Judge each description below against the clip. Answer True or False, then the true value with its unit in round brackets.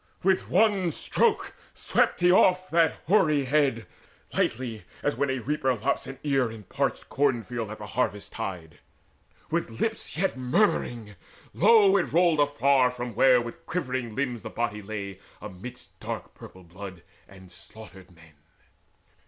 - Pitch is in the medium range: False (125 Hz)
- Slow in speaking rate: False (150 wpm)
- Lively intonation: True (6.5 semitones)